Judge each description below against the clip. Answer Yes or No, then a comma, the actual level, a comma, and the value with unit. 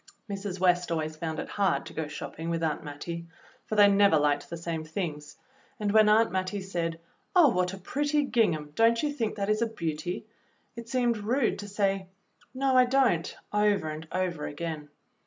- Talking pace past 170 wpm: Yes, average, 190 wpm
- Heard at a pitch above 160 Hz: Yes, high, 190 Hz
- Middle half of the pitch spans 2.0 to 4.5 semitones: No, average, 5.0 semitones